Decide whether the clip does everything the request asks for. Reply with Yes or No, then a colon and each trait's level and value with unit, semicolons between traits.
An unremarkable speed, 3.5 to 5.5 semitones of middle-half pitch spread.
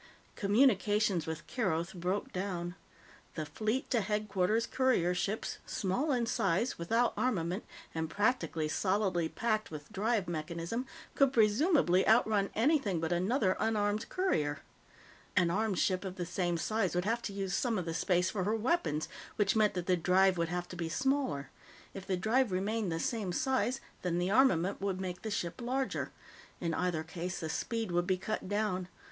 Yes: average, 170 wpm; average, 4.1 semitones